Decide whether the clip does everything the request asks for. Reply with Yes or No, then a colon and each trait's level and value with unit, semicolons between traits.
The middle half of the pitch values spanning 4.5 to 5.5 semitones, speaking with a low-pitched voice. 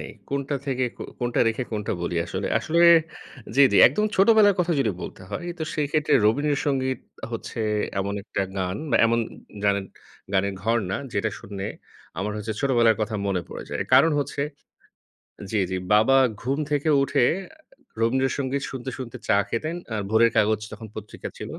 Yes: average, 5.0 semitones; low, 115 Hz